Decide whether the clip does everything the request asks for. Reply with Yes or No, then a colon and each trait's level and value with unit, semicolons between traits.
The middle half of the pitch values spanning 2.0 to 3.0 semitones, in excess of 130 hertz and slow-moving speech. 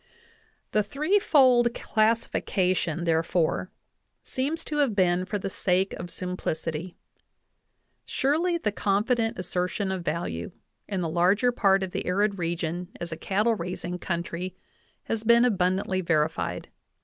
No: average, 4.3 semitones; medium, 185 Hz; slow, 125 wpm